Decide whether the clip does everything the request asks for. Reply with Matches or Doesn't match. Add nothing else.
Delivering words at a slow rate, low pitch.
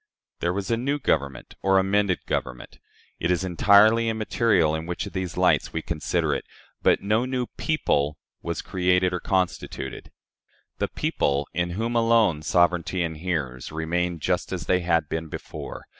Doesn't match